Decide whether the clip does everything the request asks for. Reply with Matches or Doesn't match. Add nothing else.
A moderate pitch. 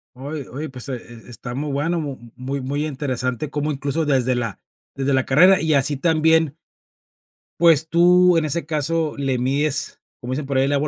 Matches